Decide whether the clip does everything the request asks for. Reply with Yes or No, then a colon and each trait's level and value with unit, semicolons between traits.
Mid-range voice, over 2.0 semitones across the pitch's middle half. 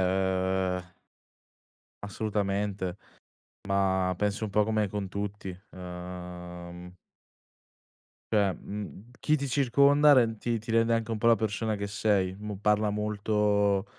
No: low, 105 Hz; narrow, 2.6 semitones